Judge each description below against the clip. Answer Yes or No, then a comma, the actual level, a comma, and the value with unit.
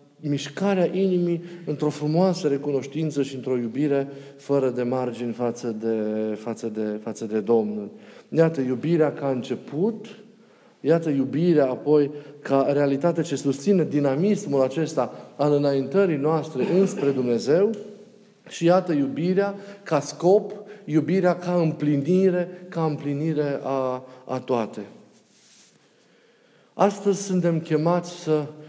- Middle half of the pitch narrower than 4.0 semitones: No, average, 4.9 semitones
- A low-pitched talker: No, medium, 150 Hz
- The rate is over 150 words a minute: No, slow, 115 wpm